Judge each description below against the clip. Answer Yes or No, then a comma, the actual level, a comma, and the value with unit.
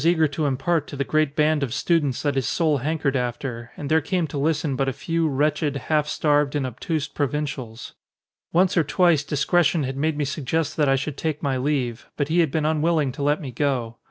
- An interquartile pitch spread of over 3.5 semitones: No, narrow, 2.6 semitones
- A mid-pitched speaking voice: Yes, medium, 145 Hz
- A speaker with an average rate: No, fast, 225 wpm